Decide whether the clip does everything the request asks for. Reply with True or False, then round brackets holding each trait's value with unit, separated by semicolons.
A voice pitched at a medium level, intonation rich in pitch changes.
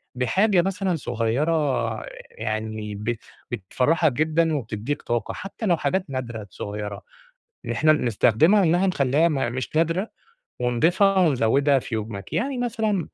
True (145 Hz; 7.0 semitones)